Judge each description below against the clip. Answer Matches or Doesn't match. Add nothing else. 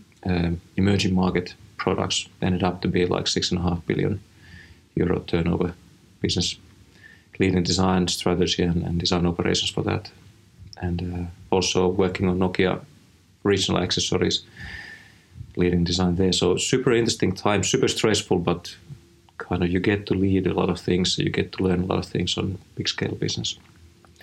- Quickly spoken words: Doesn't match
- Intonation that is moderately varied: Doesn't match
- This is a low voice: Matches